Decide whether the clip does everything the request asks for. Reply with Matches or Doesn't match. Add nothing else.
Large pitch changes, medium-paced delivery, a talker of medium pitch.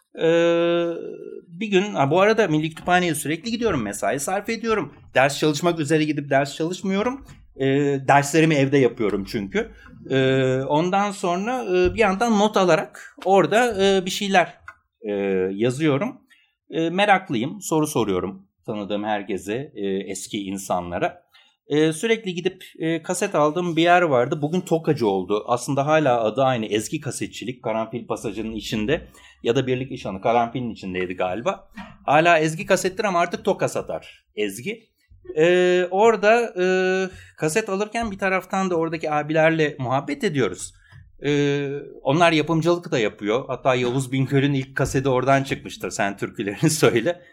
Matches